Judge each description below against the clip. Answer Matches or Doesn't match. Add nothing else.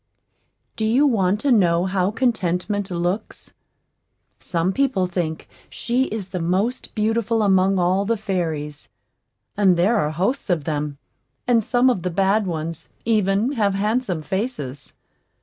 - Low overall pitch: Doesn't match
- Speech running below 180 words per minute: Matches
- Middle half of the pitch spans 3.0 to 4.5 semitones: Matches